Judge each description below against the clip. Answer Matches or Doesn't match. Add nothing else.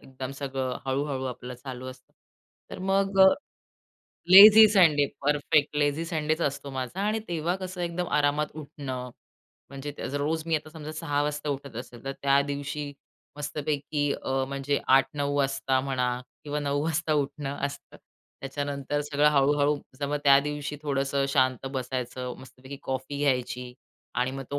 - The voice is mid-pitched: Matches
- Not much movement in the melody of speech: Matches